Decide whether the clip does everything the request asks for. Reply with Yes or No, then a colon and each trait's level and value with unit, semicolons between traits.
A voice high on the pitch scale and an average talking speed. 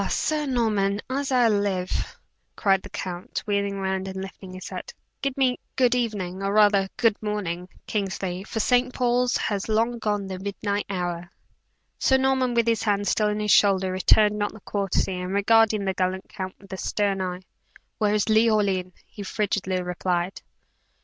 Yes: high, 205 Hz; average, 170 wpm